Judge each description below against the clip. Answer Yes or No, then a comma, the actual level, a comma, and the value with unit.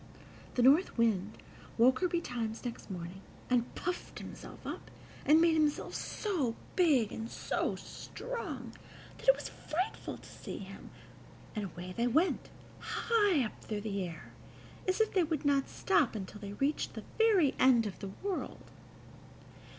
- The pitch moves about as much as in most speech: No, wide, 8.3 semitones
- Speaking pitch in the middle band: No, very high, 260 Hz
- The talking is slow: No, average, 160 wpm